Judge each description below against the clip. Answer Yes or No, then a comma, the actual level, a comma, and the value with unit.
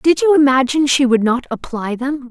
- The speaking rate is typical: No, fast, 210 wpm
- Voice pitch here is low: No, very high, 270 Hz